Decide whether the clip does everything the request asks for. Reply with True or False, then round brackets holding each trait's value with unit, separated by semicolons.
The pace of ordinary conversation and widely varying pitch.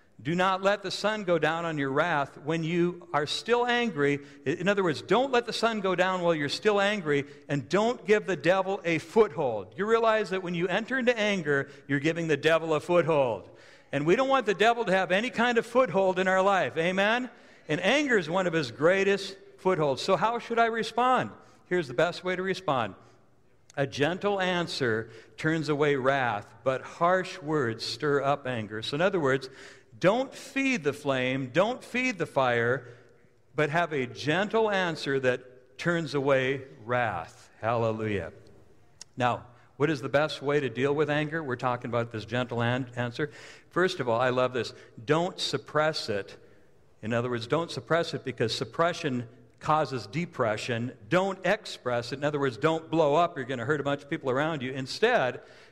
True (185 wpm; 6.3 semitones)